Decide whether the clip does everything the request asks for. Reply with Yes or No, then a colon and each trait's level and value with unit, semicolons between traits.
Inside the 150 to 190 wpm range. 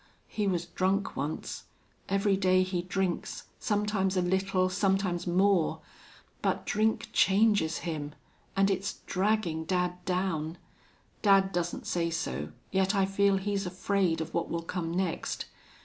No: slow, 135 wpm